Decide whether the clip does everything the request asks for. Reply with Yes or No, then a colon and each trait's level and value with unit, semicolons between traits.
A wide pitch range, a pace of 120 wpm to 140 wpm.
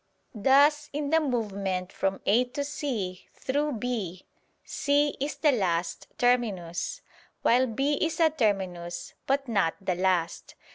Yes: wide, 7.2 semitones; slow, 135 wpm